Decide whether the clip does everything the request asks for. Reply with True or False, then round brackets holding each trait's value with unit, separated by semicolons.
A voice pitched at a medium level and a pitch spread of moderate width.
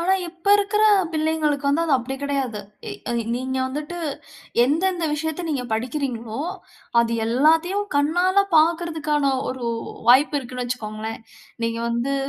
False (285 Hz; 4.5 semitones)